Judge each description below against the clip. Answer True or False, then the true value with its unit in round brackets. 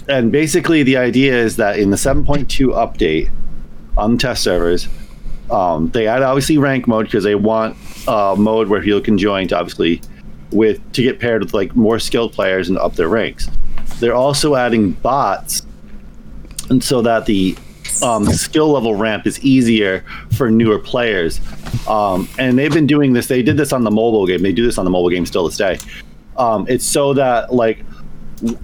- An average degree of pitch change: True (4.7 semitones)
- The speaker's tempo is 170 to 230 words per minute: True (185 wpm)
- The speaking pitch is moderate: False (115 Hz)